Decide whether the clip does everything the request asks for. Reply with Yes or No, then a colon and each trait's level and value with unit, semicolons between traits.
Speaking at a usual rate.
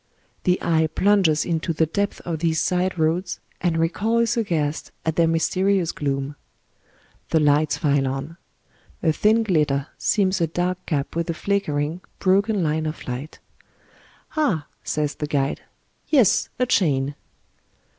Yes: average, 145 wpm